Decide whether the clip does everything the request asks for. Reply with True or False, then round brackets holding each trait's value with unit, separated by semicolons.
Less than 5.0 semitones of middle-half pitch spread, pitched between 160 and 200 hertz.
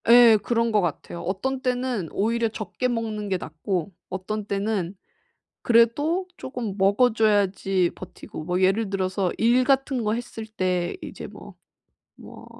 False (3.8 semitones; 215 Hz)